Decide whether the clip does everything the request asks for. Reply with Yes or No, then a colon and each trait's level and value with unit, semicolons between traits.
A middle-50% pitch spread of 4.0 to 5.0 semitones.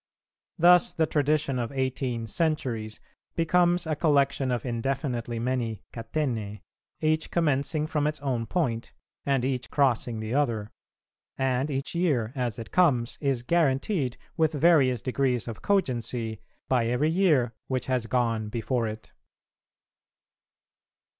Yes: average, 4.5 semitones